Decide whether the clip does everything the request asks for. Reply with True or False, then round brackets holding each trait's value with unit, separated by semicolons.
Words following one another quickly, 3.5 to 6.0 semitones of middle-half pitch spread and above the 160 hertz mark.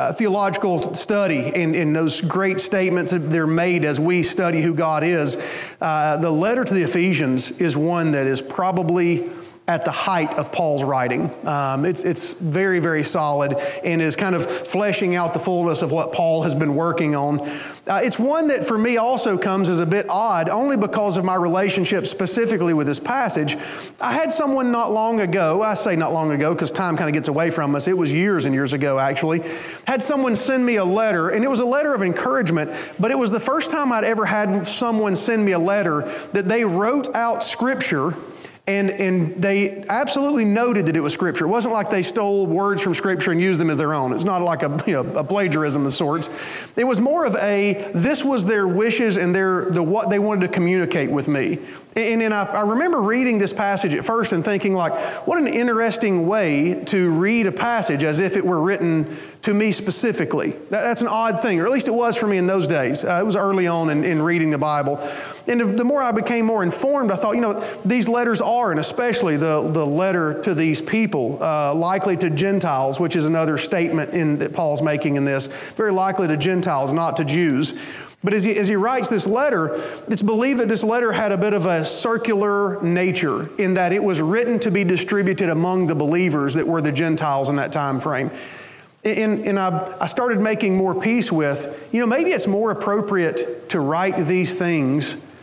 True (215 wpm; 4.9 semitones; 185 Hz)